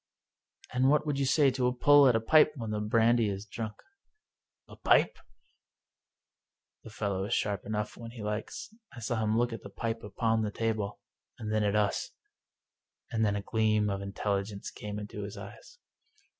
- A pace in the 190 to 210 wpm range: Yes, average, 200 wpm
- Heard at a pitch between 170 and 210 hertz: No, low, 110 Hz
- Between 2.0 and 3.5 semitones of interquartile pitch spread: Yes, narrow, 2.4 semitones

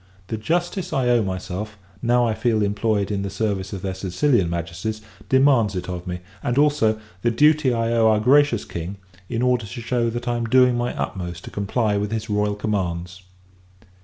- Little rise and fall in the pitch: No, average, 3.7 semitones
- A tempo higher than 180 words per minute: Yes, average, 190 wpm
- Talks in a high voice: No, low, 110 Hz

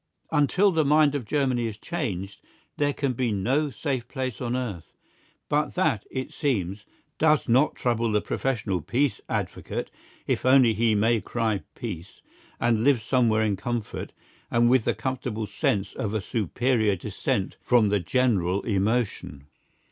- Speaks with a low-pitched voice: Yes, low, 120 Hz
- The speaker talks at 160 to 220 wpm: No, average, 150 wpm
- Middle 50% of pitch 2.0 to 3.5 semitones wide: No, average, 4.1 semitones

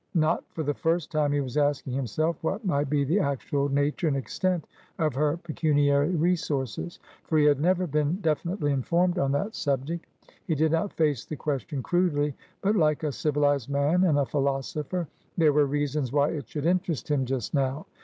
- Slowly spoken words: No, average, 185 wpm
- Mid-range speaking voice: Yes, medium, 150 Hz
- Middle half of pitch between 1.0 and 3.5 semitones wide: Yes, average, 2.8 semitones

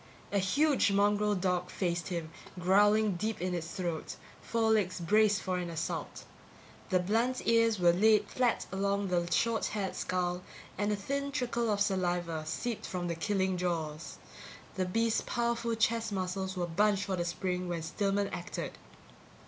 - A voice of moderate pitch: No, high, 195 Hz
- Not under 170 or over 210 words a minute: No, average, 155 wpm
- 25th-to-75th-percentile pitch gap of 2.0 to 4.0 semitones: Yes, average, 3.4 semitones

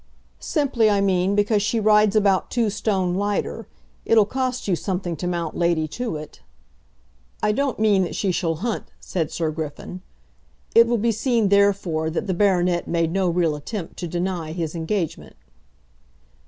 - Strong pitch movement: No, average, 3.8 semitones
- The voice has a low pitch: No, high, 190 Hz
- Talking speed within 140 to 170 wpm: Yes, average, 160 wpm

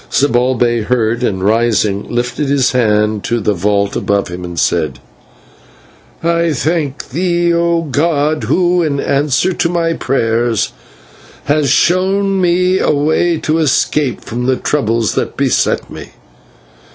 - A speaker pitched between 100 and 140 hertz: Yes, low, 135 Hz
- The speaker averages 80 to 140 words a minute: Yes, slow, 135 wpm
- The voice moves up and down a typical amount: No, wide, 6.6 semitones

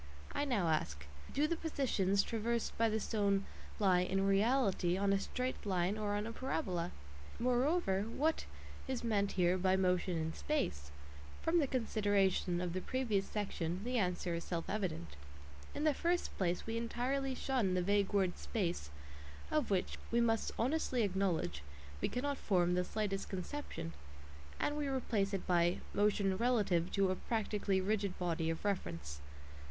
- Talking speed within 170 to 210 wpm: No, average, 160 wpm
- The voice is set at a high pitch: Yes, high, 200 Hz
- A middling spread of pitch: Yes, average, 4.8 semitones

